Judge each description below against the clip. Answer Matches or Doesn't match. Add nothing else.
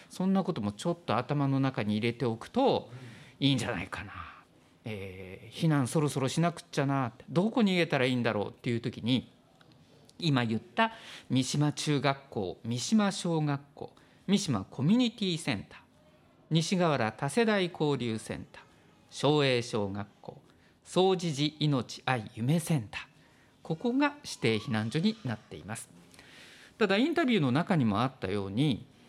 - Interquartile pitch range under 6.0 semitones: Doesn't match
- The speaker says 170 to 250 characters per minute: Doesn't match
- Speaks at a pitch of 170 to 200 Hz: Doesn't match